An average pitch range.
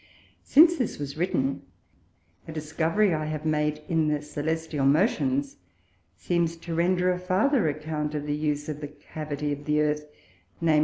No: narrow, 2.1 semitones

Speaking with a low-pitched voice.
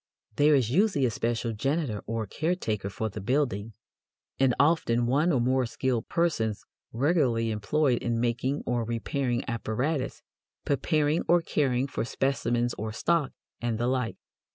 Yes: low, 125 Hz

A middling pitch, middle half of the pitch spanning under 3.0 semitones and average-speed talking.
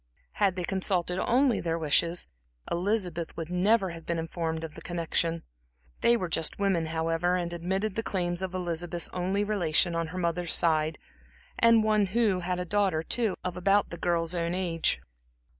Yes: medium, 175 Hz; narrow, 2.5 semitones; average, 175 wpm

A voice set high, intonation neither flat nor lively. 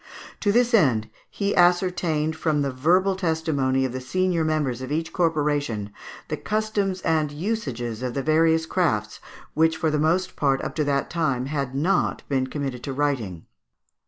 No: medium, 155 Hz; average, 4.8 semitones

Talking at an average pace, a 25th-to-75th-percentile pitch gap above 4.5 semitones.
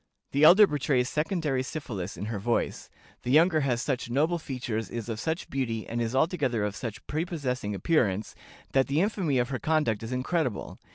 Yes: average, 180 wpm; average, 5.3 semitones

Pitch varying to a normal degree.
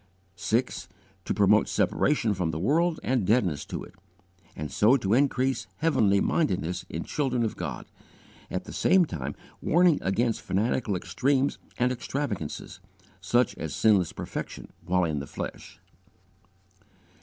No: wide, 6.6 semitones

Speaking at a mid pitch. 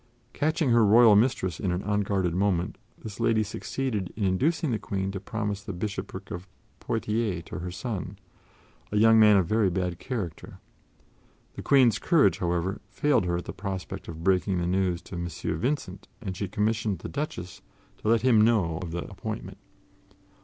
No: low, 100 Hz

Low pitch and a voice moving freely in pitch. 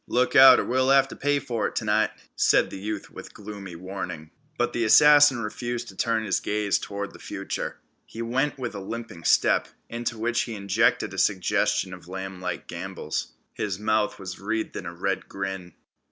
No: low, 105 Hz; average, 3.8 semitones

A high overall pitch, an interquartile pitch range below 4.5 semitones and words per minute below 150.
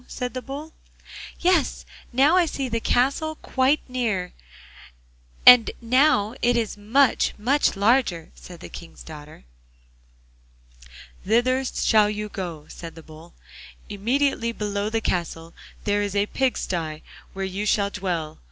No: high, 215 Hz; wide, 5.6 semitones; slow, 135 wpm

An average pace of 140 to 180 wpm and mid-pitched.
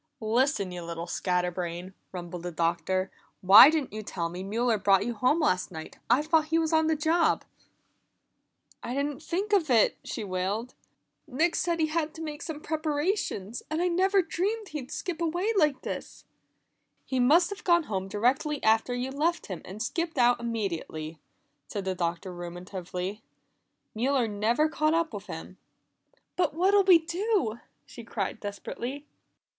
No: average, 165 wpm; high, 245 Hz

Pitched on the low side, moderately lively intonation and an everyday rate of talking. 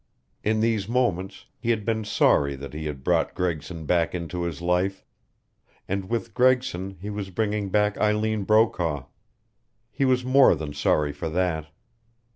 Yes: very low, 95 Hz; average, 4.7 semitones; average, 155 wpm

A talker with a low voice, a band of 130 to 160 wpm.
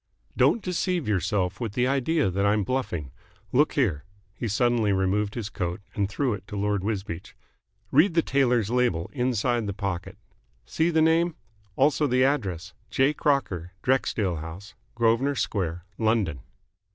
Yes: low, 110 Hz; average, 150 wpm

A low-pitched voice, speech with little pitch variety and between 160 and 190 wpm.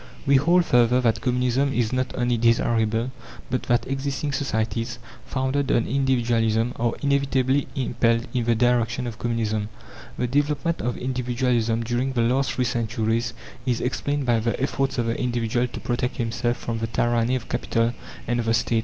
Yes: low, 120 Hz; narrow, 2.1 semitones; average, 170 wpm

